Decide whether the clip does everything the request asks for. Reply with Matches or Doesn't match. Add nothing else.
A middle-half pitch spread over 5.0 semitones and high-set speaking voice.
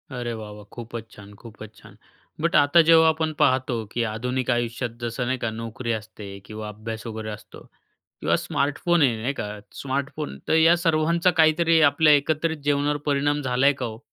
Doesn't match